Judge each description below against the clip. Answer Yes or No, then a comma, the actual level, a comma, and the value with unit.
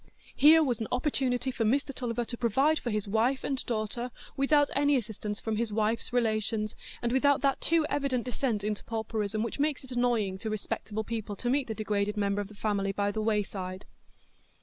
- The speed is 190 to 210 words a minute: Yes, average, 195 wpm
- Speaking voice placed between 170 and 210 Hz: No, high, 230 Hz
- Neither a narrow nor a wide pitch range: Yes, average, 3.7 semitones